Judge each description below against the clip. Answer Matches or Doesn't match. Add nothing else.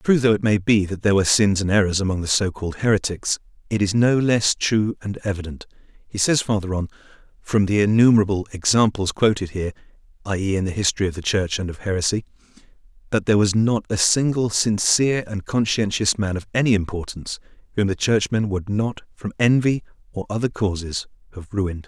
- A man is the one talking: Matches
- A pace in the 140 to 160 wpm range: Doesn't match